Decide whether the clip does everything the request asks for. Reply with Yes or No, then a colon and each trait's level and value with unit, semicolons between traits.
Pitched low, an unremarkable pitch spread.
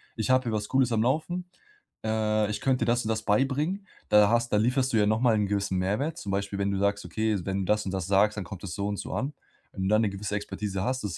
Yes: low, 105 Hz; average, 3.4 semitones